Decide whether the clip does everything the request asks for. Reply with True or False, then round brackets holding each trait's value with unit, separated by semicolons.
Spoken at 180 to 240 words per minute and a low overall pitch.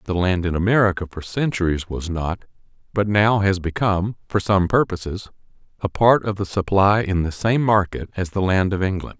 True (190 wpm; 95 Hz)